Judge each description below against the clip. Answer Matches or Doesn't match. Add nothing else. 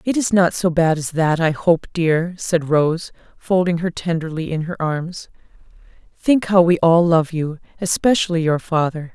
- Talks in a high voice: Doesn't match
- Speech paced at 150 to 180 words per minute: Matches